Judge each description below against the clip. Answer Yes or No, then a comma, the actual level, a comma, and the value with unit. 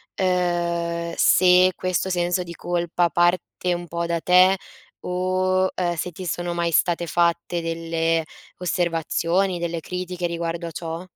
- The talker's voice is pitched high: No, medium, 175 Hz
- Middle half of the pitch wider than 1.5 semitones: No, narrow, 1.2 semitones